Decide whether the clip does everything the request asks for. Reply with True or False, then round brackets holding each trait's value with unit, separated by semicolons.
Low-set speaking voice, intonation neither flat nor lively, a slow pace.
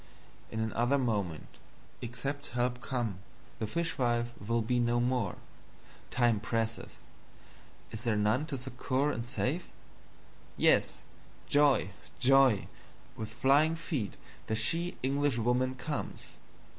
True (120 Hz; 3.3 semitones; 110 wpm)